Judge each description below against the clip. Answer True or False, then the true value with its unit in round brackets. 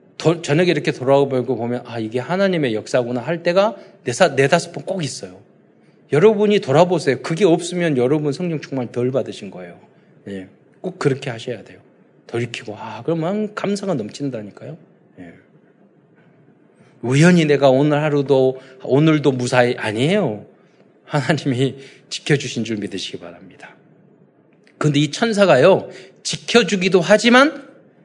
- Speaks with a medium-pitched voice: True (145 Hz)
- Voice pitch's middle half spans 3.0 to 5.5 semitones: False (6.0 semitones)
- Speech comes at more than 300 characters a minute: True (310 characters per minute)